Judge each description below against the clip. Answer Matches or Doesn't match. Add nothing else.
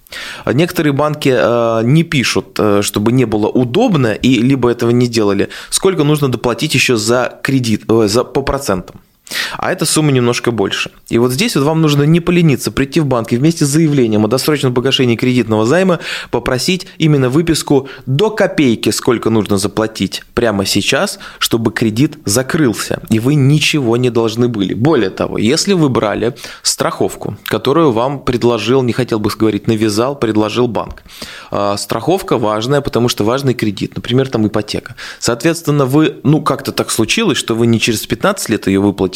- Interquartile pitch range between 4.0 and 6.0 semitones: Matches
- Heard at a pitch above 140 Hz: Doesn't match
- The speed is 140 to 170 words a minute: Matches